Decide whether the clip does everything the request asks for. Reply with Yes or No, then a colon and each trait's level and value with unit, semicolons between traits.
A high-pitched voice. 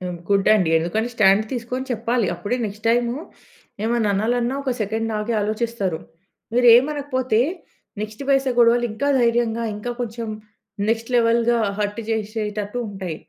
Yes: high, 230 Hz